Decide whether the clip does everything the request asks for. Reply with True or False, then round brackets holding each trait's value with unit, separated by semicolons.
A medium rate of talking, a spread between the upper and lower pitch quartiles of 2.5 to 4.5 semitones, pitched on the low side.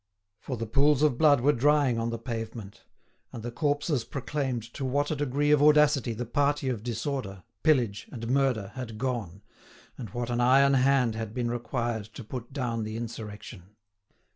True (175 wpm; 3.6 semitones; 125 Hz)